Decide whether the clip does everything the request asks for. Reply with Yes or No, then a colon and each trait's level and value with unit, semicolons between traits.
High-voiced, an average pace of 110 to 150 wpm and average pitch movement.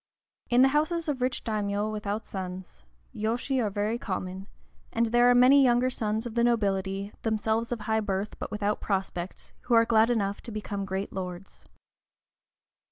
No: high, 215 Hz; average, 165 wpm; average, 3.3 semitones